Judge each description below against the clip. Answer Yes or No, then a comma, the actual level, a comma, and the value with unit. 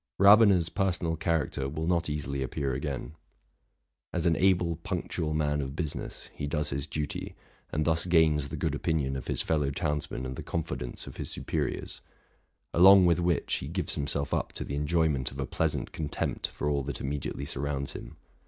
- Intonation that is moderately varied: Yes, average, 3.0 semitones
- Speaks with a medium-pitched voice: No, very low, 75 Hz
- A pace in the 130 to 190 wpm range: Yes, average, 180 wpm